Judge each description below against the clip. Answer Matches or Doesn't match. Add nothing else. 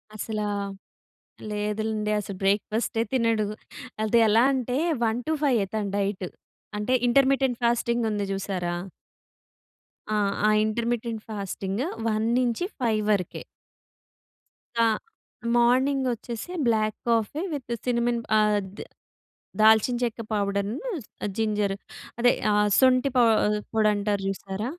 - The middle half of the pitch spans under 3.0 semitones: Matches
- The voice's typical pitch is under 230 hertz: Matches